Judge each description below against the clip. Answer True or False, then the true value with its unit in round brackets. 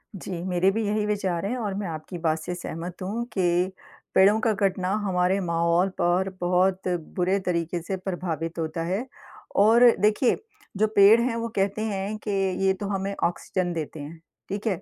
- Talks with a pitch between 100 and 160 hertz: False (190 Hz)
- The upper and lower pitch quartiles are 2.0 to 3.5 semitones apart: True (2.7 semitones)